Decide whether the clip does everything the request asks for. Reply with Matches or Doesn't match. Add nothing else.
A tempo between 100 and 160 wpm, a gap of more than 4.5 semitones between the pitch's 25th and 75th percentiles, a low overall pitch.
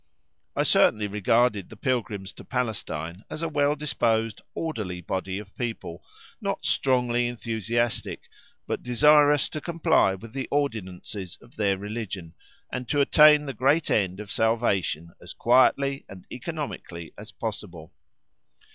Matches